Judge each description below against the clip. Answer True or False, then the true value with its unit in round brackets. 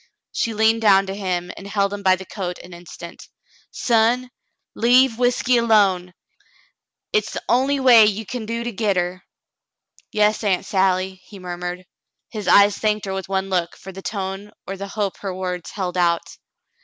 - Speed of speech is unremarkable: True (175 wpm)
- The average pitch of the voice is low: False (200 Hz)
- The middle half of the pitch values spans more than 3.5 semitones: False (3.0 semitones)